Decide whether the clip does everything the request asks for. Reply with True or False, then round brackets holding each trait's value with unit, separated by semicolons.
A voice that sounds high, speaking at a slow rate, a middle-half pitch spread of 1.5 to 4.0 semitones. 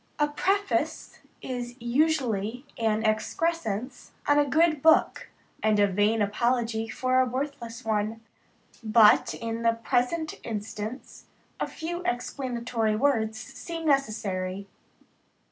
False (240 Hz; 110 wpm; 4.4 semitones)